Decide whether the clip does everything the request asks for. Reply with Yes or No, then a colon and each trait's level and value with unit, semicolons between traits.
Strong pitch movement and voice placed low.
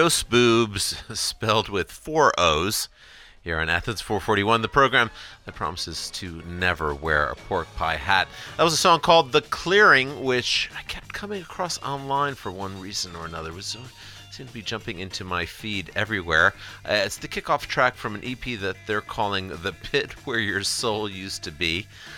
Yes: wide, 5.7 semitones; low, 105 Hz